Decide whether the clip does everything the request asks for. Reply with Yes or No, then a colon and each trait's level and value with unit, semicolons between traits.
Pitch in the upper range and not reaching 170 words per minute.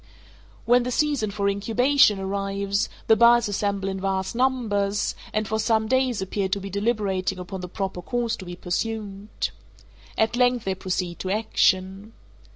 Yes: high, 200 Hz; average, 160 wpm